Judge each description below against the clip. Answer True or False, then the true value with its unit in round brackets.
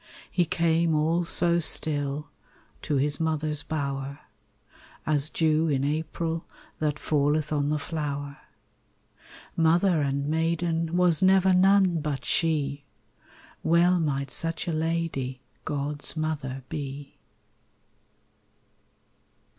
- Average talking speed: False (105 wpm)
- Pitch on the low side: False (155 Hz)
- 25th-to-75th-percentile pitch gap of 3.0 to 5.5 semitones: False (2.5 semitones)